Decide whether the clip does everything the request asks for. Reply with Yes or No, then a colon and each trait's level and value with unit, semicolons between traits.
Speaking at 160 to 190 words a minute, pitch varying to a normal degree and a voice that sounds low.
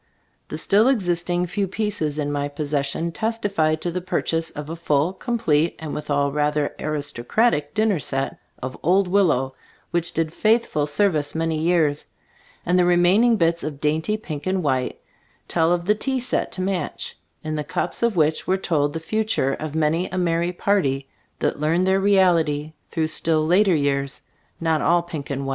No: average, 180 wpm; average, 4.0 semitones; medium, 165 Hz